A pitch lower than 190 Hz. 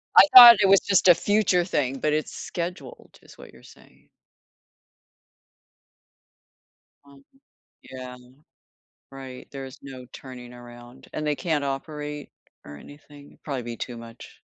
Yes: medium, 140 Hz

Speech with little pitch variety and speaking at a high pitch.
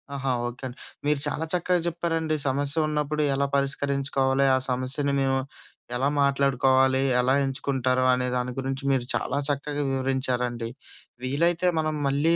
No: narrow, 2.0 semitones; low, 135 Hz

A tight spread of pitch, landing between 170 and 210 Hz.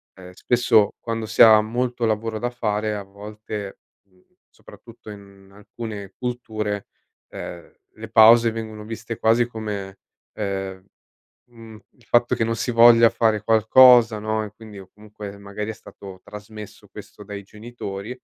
No: narrow, 2.0 semitones; low, 110 Hz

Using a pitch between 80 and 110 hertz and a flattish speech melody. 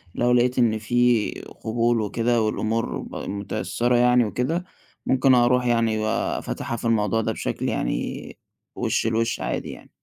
No: low, 120 Hz; narrow, 1.8 semitones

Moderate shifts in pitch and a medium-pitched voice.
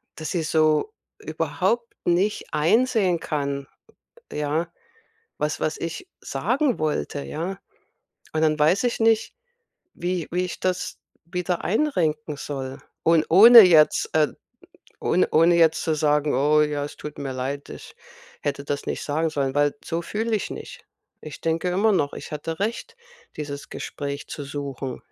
Yes: average, 3.8 semitones; medium, 155 Hz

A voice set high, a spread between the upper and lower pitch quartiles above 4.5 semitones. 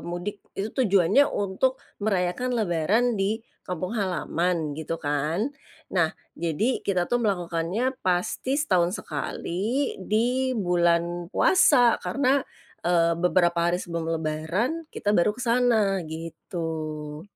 No: medium, 180 Hz; average, 5.1 semitones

